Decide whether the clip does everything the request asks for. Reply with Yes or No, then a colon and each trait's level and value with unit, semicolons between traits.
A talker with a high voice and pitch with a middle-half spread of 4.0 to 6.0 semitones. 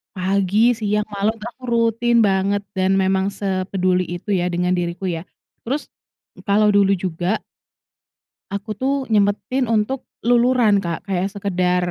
No: high, 200 Hz; average, 2.9 semitones